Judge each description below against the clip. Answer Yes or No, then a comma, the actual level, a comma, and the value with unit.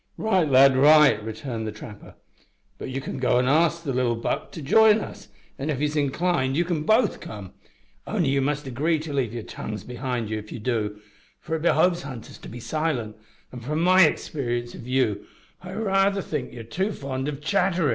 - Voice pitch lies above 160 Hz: No, medium, 140 Hz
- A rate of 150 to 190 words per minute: No, average, 200 wpm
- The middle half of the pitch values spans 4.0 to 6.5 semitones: Yes, wide, 5.5 semitones